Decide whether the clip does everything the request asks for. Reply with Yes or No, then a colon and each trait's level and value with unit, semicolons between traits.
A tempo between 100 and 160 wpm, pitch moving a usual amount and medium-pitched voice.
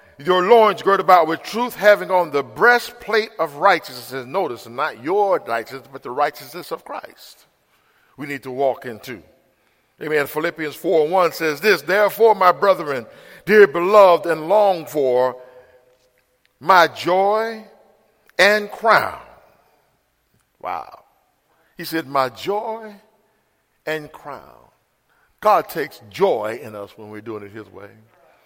No: slow, 135 wpm; wide, 7.6 semitones; medium, 165 Hz